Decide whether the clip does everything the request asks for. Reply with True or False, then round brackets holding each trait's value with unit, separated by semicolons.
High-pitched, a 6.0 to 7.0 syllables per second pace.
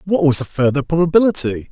False (155 Hz; 6.3 syllables/s)